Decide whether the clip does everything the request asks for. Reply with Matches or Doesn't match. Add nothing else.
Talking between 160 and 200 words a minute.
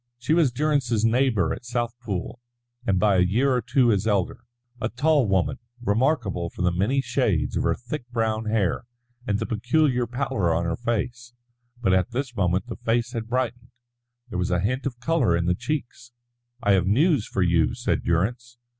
Matches